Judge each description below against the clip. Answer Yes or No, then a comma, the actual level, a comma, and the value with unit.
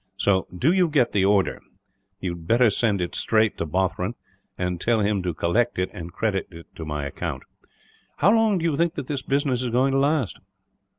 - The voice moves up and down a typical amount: No, wide, 7.0 semitones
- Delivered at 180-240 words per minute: Yes, fast, 205 wpm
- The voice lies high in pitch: No, low, 110 Hz